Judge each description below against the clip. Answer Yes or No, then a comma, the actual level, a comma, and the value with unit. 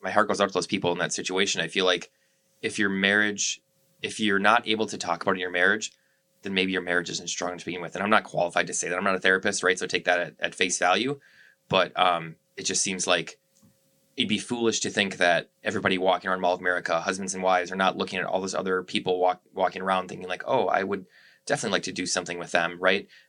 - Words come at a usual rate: No, fast, 260 wpm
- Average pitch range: No, narrow, 1.7 semitones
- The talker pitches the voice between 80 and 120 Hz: Yes, very low, 95 Hz